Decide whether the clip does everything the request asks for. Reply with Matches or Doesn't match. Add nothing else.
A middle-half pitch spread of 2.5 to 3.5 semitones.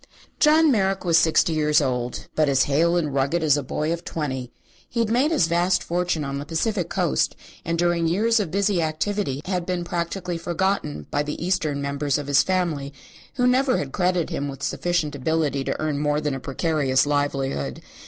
Doesn't match